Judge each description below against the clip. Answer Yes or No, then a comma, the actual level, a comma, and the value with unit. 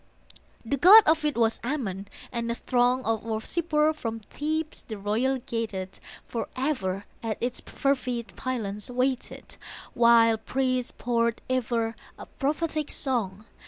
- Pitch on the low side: No, high, 245 Hz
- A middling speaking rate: No, slow, 125 wpm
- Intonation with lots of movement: No, average, 3.3 semitones